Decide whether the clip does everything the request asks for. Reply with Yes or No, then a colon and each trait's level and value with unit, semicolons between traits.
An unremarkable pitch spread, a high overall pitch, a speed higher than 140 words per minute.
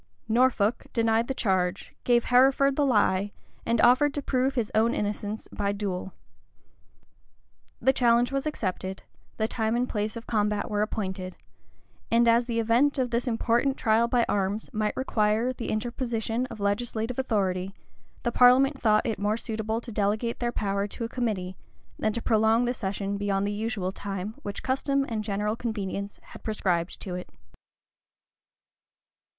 Yes: average, 3.0 semitones; high, 220 Hz; average, 160 wpm